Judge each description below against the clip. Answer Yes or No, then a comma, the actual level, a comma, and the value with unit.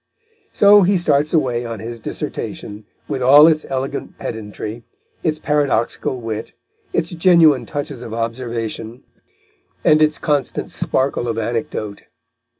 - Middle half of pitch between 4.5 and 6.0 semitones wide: Yes, average, 5.0 semitones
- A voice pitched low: Yes, low, 130 Hz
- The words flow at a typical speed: No, slow, 125 wpm